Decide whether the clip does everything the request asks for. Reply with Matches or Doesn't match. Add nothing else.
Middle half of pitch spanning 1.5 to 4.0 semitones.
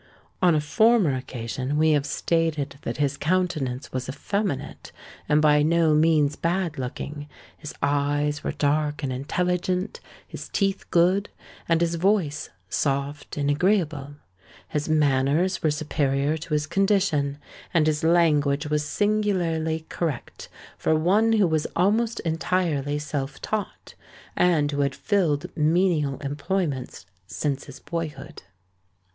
Matches